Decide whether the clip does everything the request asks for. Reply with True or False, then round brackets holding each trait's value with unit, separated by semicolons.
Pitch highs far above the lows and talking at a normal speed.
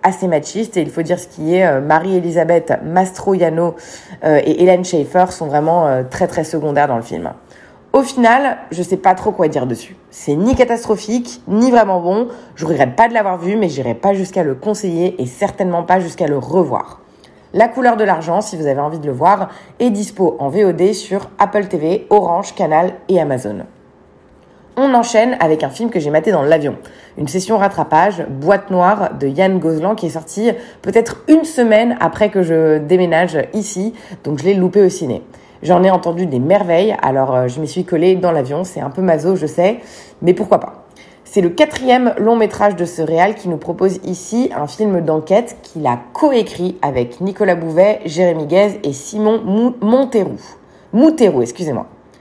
False (4.4 semitones; 185 wpm)